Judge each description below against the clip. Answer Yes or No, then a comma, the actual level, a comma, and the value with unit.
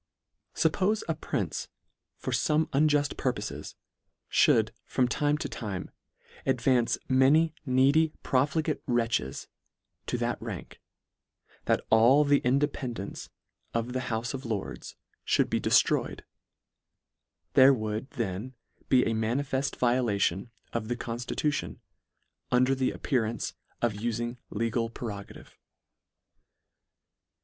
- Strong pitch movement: No, average, 3.3 semitones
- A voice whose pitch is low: Yes, low, 125 Hz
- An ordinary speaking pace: No, slow, 110 wpm